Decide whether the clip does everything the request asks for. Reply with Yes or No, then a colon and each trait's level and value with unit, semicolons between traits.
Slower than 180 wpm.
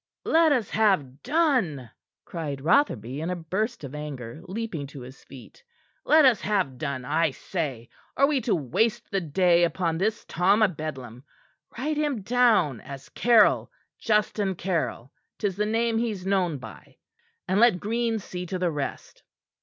Yes: average, 160 wpm